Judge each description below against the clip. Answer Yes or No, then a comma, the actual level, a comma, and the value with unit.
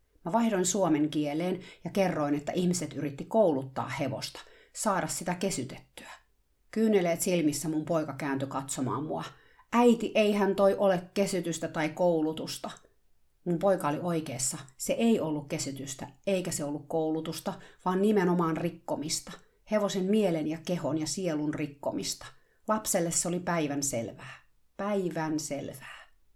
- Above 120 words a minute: Yes, average, 130 wpm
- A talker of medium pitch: Yes, medium, 170 Hz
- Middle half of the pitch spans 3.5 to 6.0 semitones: Yes, average, 4.4 semitones